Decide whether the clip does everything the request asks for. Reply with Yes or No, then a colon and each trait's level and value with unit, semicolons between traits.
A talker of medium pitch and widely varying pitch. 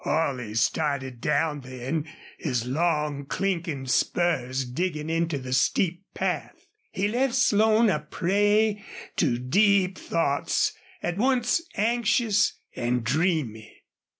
Yes: medium, 160 Hz; wide, 7.1 semitones